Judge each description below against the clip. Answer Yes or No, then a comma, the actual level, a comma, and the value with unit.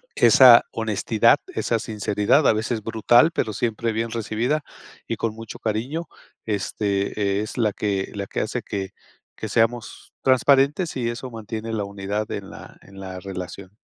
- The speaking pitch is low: Yes, low, 110 Hz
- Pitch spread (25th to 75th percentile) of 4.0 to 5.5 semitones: No, average, 2.7 semitones